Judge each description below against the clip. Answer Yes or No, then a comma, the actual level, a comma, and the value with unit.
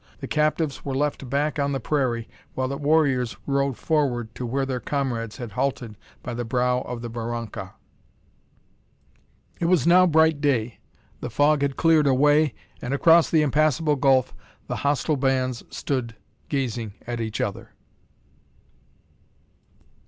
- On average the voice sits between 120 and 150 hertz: Yes, low, 135 Hz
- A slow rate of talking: No, average, 145 wpm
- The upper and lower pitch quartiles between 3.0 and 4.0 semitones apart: Yes, average, 3.6 semitones